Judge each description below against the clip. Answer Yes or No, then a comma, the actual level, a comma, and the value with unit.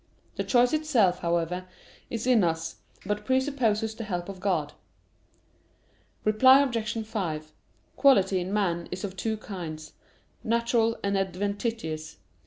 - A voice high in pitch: Yes, high, 205 Hz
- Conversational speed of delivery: No, slow, 125 wpm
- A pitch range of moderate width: Yes, average, 4.5 semitones